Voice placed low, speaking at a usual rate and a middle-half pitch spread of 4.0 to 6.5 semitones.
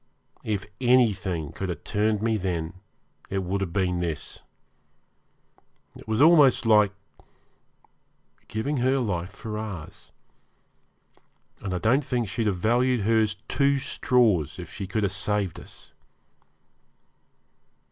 No: low, 105 Hz; slow, 125 wpm; average, 4.3 semitones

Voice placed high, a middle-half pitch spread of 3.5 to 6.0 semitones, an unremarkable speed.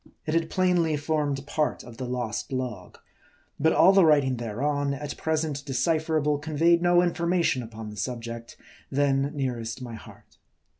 No: medium, 145 Hz; average, 4.3 semitones; average, 150 wpm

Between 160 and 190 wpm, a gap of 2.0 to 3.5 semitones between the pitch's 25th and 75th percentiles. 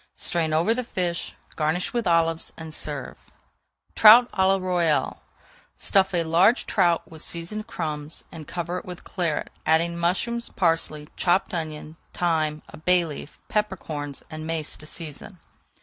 No: average, 150 wpm; average, 2.8 semitones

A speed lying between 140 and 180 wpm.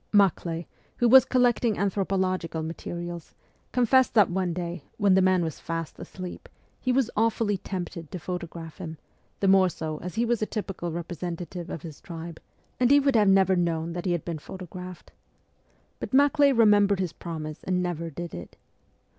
Yes: average, 170 wpm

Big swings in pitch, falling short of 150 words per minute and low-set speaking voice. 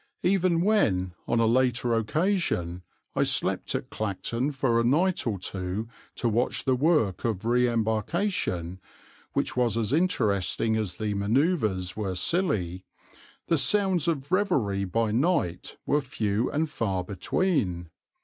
Yes: wide, 7.8 semitones; average, 140 wpm; low, 115 Hz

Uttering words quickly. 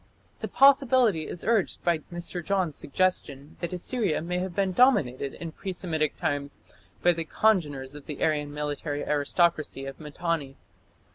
No: average, 150 wpm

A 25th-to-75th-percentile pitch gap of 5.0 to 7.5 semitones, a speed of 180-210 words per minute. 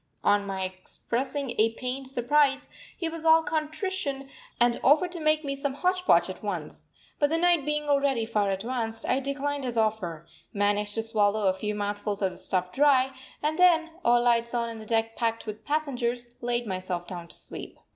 Yes: wide, 5.4 semitones; average, 190 wpm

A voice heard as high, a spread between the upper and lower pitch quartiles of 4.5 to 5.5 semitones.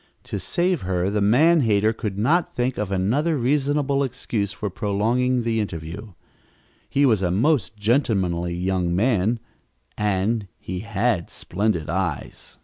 No: low, 105 Hz; average, 5.0 semitones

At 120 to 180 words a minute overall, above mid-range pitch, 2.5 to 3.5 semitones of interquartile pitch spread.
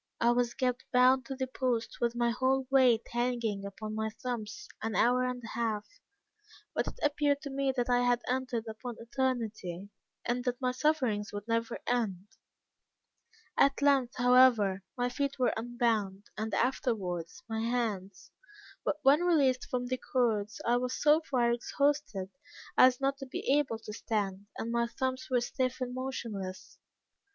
Yes: average, 160 wpm; high, 245 Hz; average, 2.8 semitones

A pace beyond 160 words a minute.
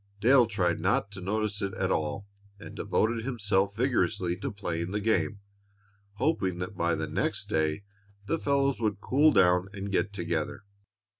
No: average, 155 wpm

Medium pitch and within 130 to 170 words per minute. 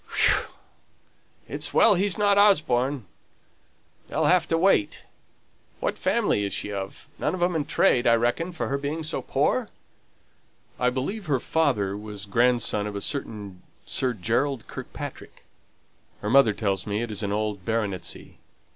No: low, 120 Hz; average, 155 wpm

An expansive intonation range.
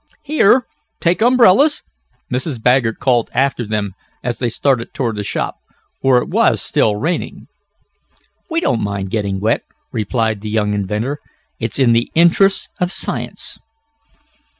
Yes: wide, 7.6 semitones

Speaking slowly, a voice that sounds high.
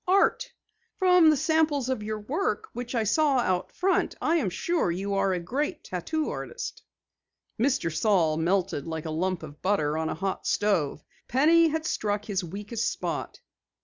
No: average, 170 wpm; high, 210 Hz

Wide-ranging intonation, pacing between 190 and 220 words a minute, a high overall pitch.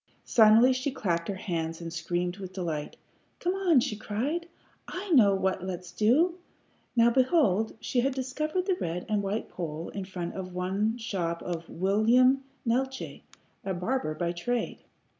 No: wide, 6.3 semitones; average, 160 wpm; high, 210 Hz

